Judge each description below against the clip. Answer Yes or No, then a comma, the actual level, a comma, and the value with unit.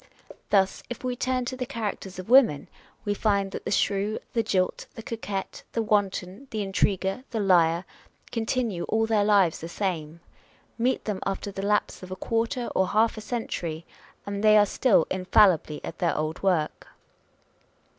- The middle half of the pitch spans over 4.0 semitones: No, average, 3.3 semitones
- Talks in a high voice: Yes, high, 200 Hz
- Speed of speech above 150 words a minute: Yes, average, 170 wpm